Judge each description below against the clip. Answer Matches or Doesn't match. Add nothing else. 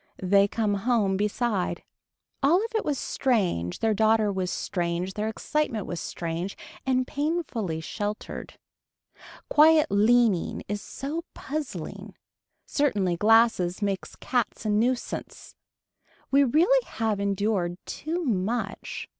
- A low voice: Doesn't match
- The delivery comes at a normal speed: Doesn't match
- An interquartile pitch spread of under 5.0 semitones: Doesn't match